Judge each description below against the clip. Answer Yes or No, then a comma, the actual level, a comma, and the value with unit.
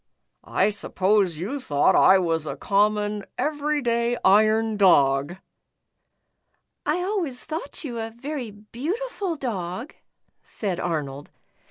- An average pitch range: No, wide, 7.1 semitones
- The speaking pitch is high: Yes, high, 215 Hz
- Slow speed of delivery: Yes, slow, 120 wpm